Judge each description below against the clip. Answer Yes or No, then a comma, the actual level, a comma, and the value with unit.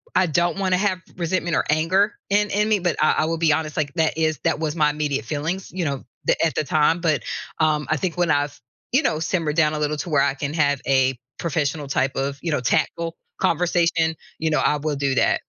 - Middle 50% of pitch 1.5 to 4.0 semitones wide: Yes, average, 2.7 semitones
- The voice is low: No, medium, 155 Hz